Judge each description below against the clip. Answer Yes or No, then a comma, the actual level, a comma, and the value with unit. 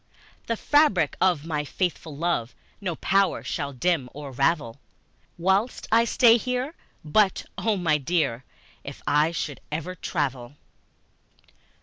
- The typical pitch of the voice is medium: Yes, medium, 170 Hz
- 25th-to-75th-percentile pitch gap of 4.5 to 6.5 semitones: Yes, average, 5.2 semitones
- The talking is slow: Yes, slow, 125 wpm